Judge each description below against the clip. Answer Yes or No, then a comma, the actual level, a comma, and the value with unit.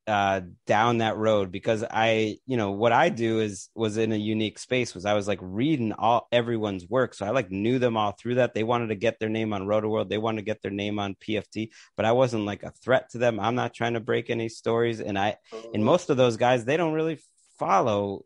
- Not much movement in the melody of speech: Yes, narrow, 2.3 semitones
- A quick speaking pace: Yes, fast, 250 wpm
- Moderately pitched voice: No, low, 110 Hz